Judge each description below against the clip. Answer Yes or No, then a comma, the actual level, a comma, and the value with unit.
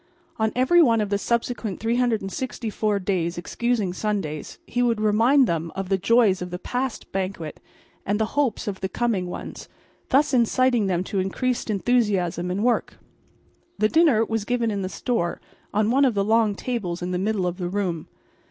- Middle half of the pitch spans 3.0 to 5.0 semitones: Yes, average, 4.3 semitones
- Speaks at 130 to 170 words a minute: No, average, 180 wpm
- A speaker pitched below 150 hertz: No, high, 215 Hz